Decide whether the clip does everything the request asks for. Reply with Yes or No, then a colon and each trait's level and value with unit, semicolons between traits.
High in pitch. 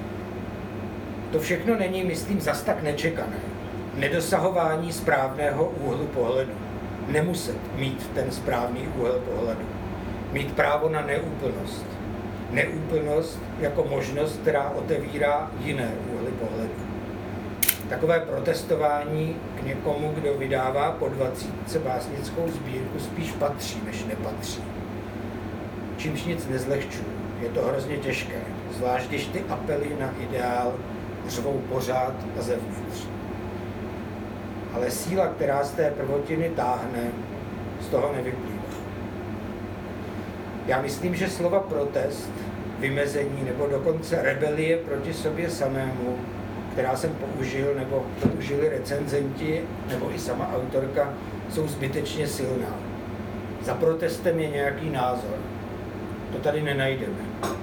No: low, 125 Hz